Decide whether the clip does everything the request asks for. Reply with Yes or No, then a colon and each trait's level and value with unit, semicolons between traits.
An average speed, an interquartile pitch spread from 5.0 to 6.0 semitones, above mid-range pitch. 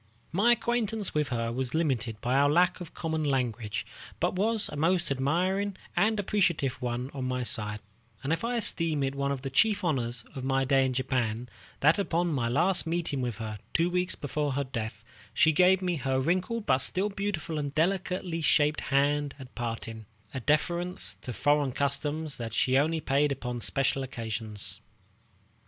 No: average, 175 wpm; wide, 5.4 semitones; medium, 145 Hz